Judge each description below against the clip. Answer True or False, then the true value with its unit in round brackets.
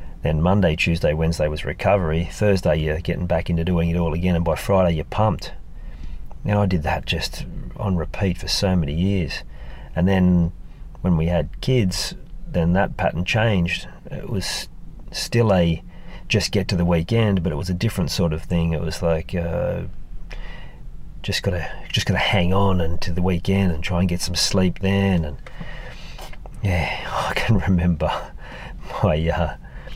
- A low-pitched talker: True (85 Hz)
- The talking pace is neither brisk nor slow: True (170 wpm)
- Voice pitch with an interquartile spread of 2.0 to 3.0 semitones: True (2.4 semitones)